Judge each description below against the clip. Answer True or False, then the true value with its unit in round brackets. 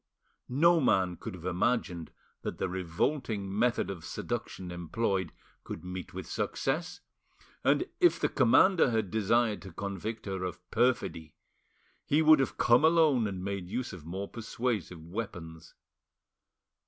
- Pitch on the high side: False (100 Hz)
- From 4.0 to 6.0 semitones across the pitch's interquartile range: True (5.5 semitones)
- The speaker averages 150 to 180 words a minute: False (140 wpm)